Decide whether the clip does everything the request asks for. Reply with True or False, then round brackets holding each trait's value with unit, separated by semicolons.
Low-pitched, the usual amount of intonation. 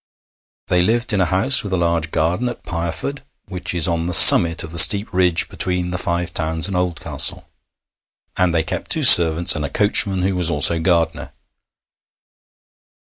False (85 Hz; 2.1 semitones)